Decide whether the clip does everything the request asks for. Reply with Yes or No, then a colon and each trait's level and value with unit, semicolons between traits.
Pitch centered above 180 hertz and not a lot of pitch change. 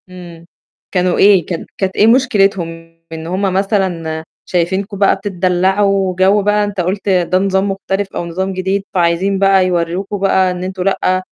Yes: high, 190 Hz; narrow, 1.8 semitones